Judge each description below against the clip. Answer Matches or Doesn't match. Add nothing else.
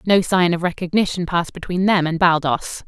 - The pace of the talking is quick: Doesn't match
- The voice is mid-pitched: Matches